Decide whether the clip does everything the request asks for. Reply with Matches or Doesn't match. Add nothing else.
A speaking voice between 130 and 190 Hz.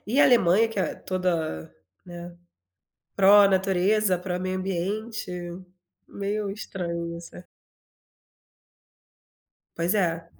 Matches